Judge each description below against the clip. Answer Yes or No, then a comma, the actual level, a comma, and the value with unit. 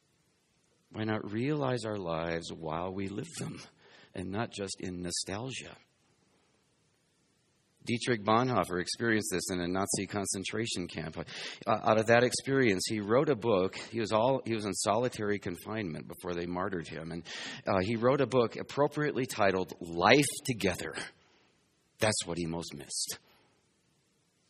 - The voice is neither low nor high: No, low, 100 Hz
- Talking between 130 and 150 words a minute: Yes, average, 145 wpm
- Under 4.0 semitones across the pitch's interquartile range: No, average, 4.7 semitones